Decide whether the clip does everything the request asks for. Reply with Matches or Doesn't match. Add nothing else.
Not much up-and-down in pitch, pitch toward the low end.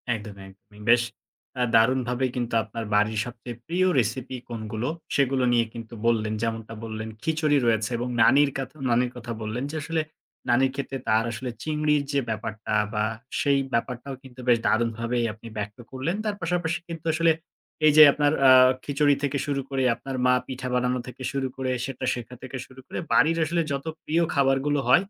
Doesn't match